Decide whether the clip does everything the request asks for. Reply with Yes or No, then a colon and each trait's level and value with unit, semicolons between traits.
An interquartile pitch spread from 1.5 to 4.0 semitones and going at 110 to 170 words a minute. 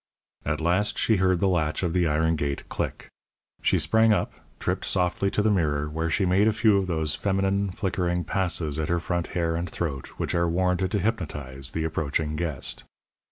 No: average, 3.6 semitones; average, 195 wpm